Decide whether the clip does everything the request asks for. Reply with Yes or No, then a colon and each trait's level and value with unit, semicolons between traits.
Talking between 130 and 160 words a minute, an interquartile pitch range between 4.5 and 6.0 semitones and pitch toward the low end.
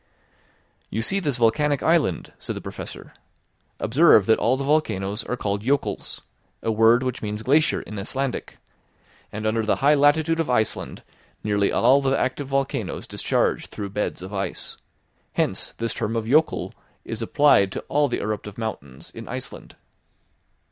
Yes: average, 155 wpm; average, 5.1 semitones; low, 115 Hz